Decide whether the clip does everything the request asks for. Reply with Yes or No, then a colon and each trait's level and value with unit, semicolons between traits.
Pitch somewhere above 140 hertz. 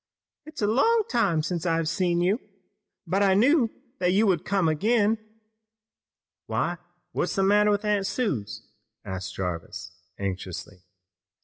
Yes: high, 190 Hz